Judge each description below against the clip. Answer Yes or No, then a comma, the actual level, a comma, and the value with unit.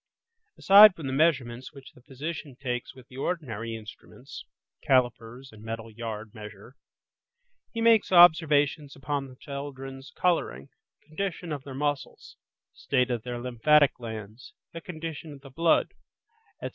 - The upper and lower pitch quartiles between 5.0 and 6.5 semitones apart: No, average, 4.2 semitones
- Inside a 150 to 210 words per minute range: No, average, 140 wpm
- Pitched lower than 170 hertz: Yes, low, 135 Hz